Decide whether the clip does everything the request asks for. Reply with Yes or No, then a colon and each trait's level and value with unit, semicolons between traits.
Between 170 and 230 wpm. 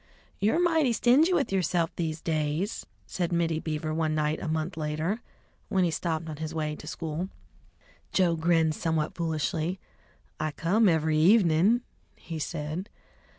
No: average, 150 wpm